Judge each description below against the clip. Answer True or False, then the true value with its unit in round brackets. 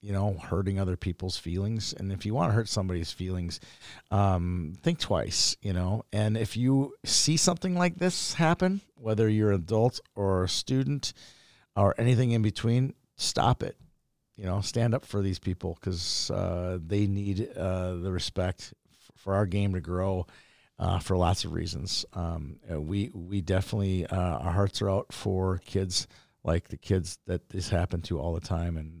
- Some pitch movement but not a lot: True (3.4 semitones)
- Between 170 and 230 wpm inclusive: True (175 wpm)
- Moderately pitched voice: False (95 Hz)